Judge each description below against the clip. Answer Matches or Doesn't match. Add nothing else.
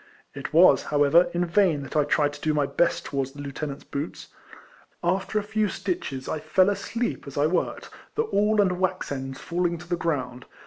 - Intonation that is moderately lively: Matches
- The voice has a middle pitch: Matches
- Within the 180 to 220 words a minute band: Matches